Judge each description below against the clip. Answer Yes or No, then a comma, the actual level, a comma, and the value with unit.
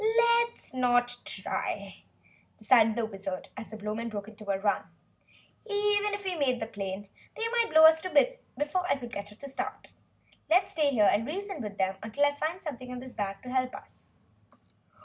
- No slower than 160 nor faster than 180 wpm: No, average, 190 wpm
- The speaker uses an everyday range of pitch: No, wide, 7.1 semitones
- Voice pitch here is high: Yes, very high, 255 Hz